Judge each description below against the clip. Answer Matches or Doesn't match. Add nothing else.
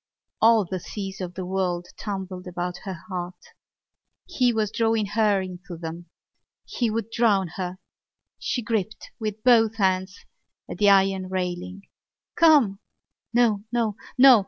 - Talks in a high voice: Matches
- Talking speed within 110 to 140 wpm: Matches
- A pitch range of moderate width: Matches